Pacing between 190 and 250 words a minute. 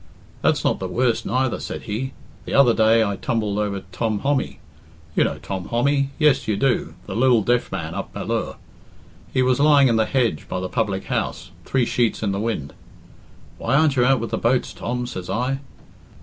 Yes: average, 195 wpm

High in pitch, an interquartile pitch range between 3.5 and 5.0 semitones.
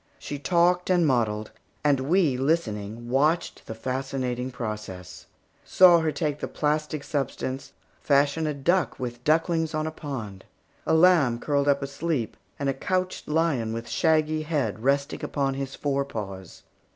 No: medium, 140 Hz; average, 4.3 semitones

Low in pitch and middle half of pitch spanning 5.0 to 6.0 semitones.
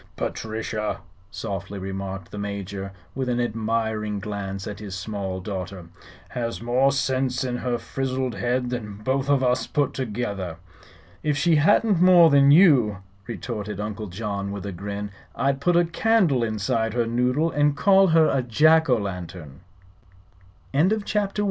Yes: low, 115 Hz; wide, 5.5 semitones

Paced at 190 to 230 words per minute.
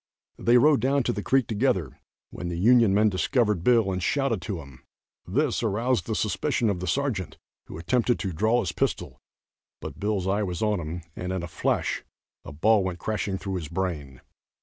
Yes: average, 195 wpm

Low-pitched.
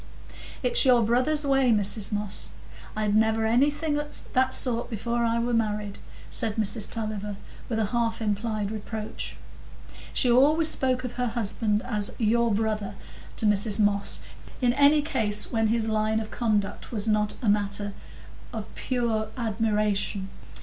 No: high, 220 Hz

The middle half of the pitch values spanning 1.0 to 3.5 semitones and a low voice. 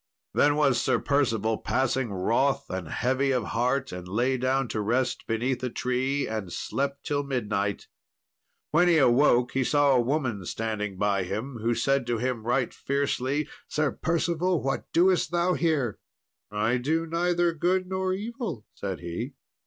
No: average, 4.7 semitones; low, 130 Hz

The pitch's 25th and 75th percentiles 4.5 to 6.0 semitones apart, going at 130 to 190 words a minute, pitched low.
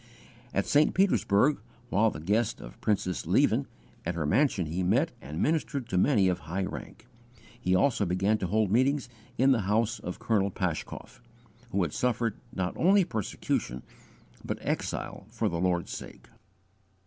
Yes: average, 5.0 semitones; average, 160 wpm; low, 100 Hz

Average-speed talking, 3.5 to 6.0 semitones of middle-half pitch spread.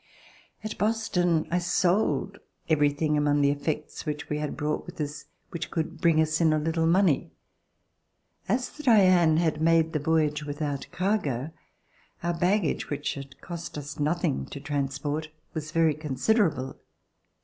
No: average, 150 wpm; average, 2.8 semitones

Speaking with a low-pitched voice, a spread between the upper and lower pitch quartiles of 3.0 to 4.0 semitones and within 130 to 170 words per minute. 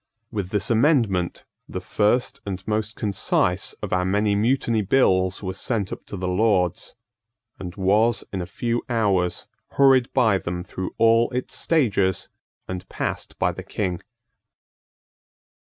Yes: low, 105 Hz; average, 3.6 semitones; average, 140 wpm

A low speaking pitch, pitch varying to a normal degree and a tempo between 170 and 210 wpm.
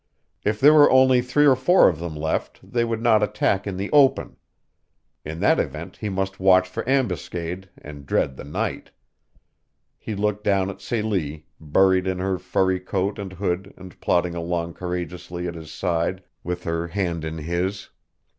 Yes: very low, 95 Hz; average, 3.3 semitones; average, 175 wpm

